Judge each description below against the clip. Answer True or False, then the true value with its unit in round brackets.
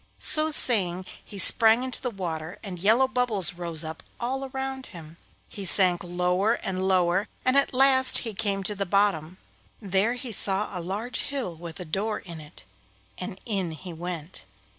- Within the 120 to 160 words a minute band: False (175 wpm)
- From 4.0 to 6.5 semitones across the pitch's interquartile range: True (5.0 semitones)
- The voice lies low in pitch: False (195 Hz)